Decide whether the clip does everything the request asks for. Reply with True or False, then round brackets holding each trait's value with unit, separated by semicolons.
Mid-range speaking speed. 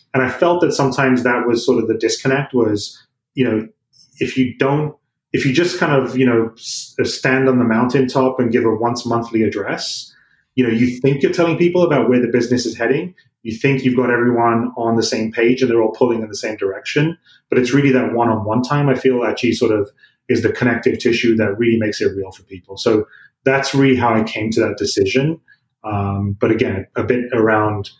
False (215 wpm)